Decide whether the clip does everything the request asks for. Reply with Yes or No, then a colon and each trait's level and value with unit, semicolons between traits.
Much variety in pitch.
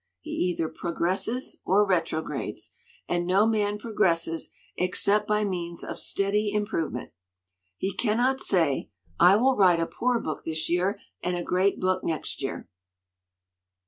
No: average, 3.7 semitones